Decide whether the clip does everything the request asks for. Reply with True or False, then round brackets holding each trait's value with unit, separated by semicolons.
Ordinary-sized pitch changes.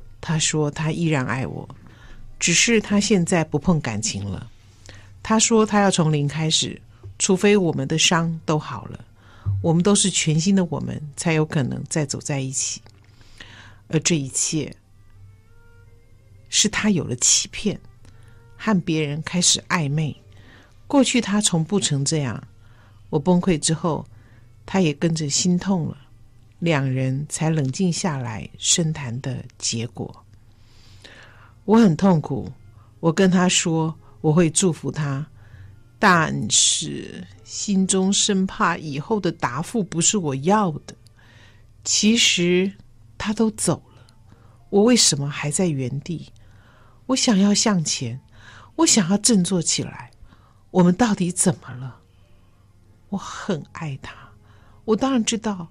False (8.3 semitones)